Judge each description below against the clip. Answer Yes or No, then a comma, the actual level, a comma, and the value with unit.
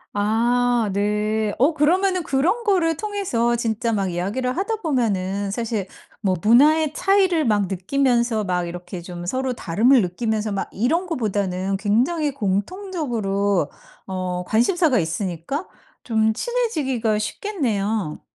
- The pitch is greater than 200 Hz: Yes, high, 230 Hz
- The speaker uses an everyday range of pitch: No, wide, 7.0 semitones